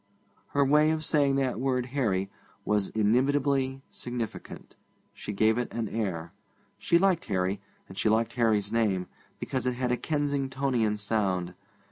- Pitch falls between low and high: No, low, 120 Hz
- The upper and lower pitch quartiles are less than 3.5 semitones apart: No, average, 4.6 semitones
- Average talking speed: Yes, average, 145 wpm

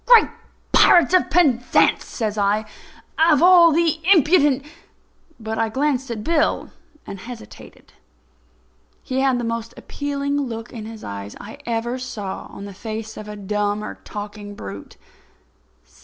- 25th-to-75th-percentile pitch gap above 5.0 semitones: Yes, wide, 5.4 semitones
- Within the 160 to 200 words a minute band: No, average, 145 wpm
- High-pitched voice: Yes, high, 230 Hz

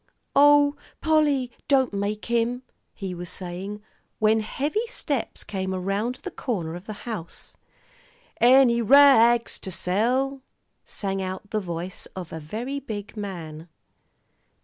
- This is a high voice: Yes, high, 215 Hz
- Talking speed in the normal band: No, slow, 130 wpm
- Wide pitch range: Yes, wide, 5.8 semitones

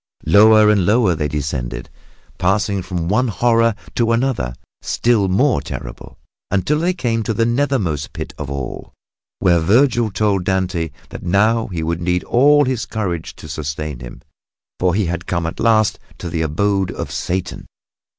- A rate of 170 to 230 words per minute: No, average, 160 wpm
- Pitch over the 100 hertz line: No, very low, 95 Hz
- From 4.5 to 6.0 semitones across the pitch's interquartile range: Yes, wide, 5.5 semitones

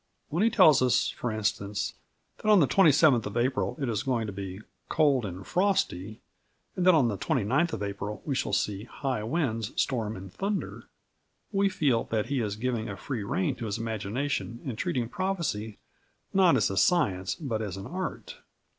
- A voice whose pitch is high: No, low, 120 Hz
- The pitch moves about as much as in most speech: No, wide, 6.8 semitones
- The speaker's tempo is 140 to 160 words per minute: No, average, 185 wpm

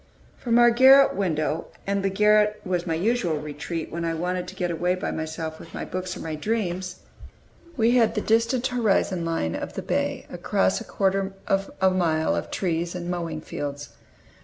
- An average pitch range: Yes, average, 4.3 semitones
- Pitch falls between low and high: Yes, medium, 180 Hz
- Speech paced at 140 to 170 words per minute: No, average, 185 wpm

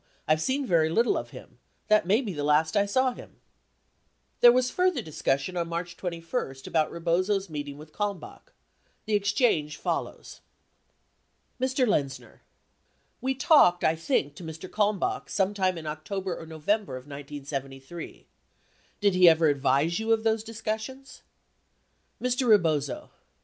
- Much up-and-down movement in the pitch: Yes, wide, 5.9 semitones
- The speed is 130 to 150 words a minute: Yes, average, 145 wpm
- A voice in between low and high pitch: Yes, medium, 180 Hz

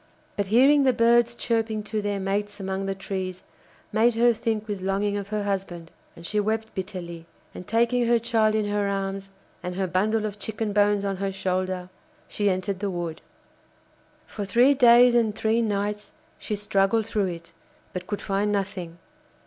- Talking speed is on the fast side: No, average, 175 wpm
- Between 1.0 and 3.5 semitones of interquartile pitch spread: Yes, narrow, 2.4 semitones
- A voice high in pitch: Yes, high, 205 Hz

